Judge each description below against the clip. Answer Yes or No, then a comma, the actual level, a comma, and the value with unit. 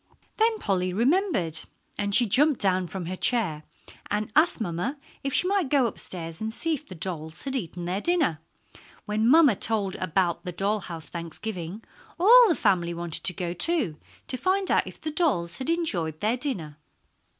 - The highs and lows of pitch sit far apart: Yes, wide, 8.5 semitones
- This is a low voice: No, high, 205 Hz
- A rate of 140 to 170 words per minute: No, average, 180 wpm